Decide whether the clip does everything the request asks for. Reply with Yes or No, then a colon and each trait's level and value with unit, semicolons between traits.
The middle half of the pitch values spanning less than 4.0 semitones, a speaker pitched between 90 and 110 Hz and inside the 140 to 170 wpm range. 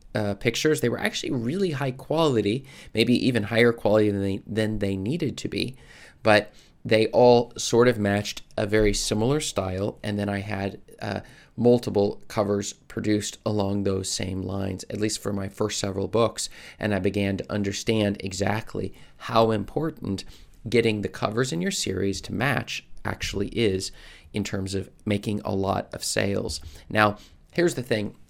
Yes: average, 2.8 semitones; low, 105 Hz; average, 165 wpm